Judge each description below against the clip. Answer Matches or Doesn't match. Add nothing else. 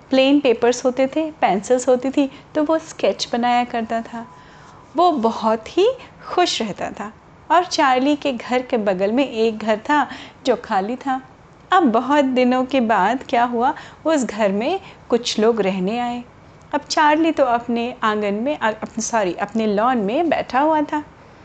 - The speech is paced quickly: Doesn't match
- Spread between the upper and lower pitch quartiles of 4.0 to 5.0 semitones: Matches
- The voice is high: Matches